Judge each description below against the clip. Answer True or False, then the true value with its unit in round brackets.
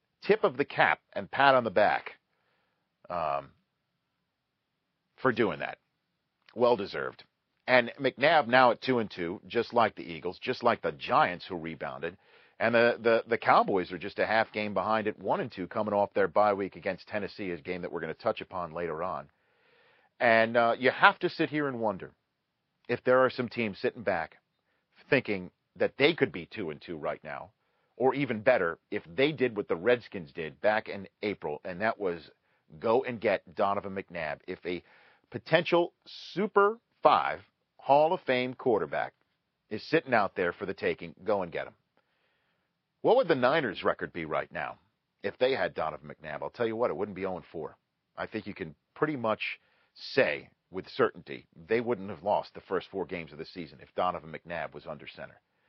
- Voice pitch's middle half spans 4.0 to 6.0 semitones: True (4.7 semitones)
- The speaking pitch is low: True (115 Hz)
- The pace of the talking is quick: False (195 wpm)